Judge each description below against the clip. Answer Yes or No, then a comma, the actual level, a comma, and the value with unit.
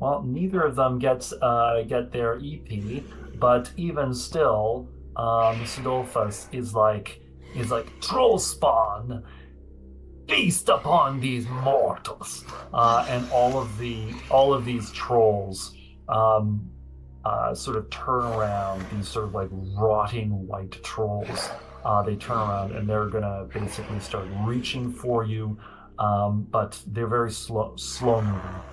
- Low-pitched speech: Yes, low, 110 Hz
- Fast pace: No, slow, 135 wpm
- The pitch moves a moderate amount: Yes, average, 3.7 semitones